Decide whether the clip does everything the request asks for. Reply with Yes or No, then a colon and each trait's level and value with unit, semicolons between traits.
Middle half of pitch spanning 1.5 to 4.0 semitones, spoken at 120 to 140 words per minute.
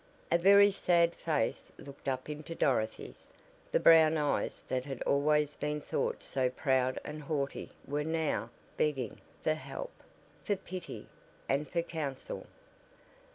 Yes: average, 3.2 semitones; slow, 135 wpm